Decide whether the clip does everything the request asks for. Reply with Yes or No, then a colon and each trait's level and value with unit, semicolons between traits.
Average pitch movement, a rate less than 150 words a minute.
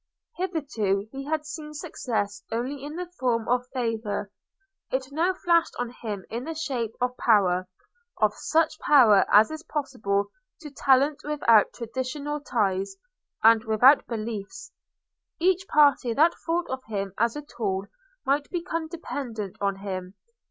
No: wide, 5.9 semitones; average, 140 wpm